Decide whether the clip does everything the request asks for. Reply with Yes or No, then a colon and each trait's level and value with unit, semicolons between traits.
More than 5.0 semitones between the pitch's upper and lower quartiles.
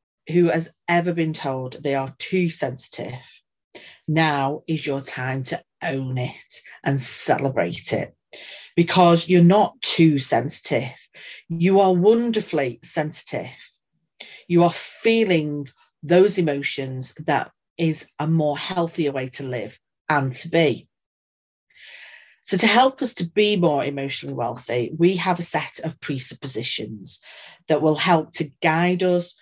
No: average, 4.1 semitones